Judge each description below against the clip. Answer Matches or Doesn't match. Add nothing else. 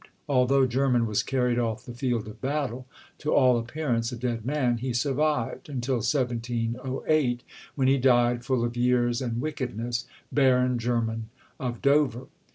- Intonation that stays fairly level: Matches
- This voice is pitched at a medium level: Doesn't match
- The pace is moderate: Matches